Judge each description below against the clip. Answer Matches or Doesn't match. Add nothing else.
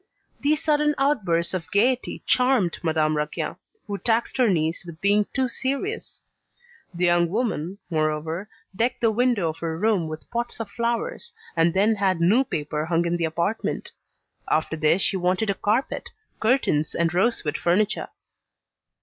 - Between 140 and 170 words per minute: Matches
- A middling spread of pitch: Doesn't match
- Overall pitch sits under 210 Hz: Matches